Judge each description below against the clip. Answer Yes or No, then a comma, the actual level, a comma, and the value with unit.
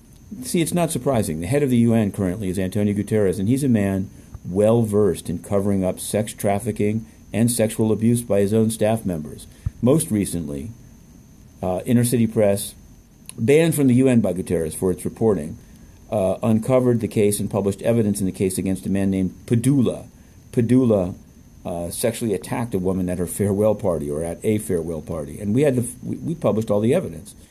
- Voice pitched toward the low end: Yes, low, 105 Hz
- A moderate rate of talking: Yes, average, 190 wpm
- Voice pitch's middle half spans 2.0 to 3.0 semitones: No, average, 3.7 semitones